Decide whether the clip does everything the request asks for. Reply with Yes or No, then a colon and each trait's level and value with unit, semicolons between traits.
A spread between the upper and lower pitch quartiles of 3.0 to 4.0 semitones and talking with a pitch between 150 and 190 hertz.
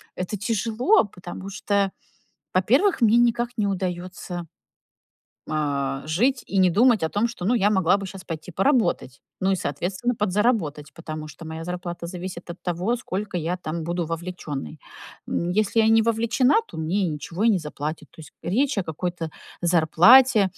No: average, 4.6 semitones; medium, 185 Hz